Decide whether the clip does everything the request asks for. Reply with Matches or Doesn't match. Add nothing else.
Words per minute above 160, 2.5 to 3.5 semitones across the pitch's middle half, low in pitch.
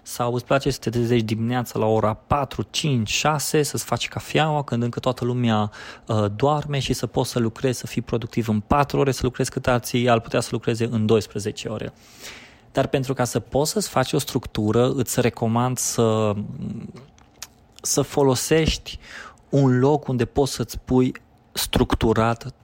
Matches